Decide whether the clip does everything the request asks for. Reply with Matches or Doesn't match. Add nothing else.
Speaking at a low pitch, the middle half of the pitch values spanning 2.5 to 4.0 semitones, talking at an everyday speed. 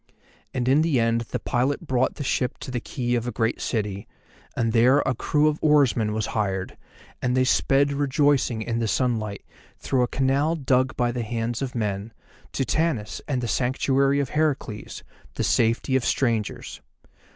Matches